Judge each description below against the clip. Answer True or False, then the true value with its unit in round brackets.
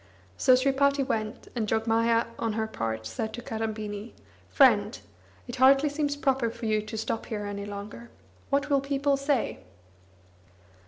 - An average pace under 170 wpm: True (150 wpm)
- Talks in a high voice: True (230 Hz)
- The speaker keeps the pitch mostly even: False (4.2 semitones)